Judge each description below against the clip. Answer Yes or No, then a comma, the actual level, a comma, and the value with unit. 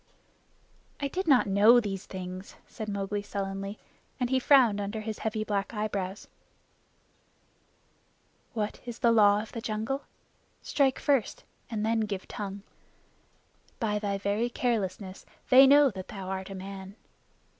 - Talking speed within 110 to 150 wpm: Yes, average, 140 wpm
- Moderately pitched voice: No, high, 210 Hz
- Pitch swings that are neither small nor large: Yes, average, 3.0 semitones